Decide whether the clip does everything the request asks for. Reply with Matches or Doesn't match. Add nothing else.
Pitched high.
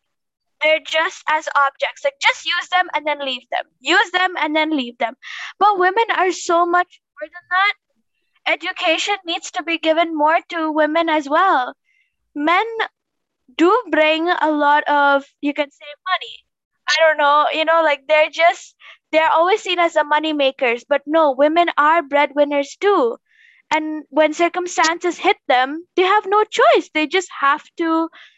Matches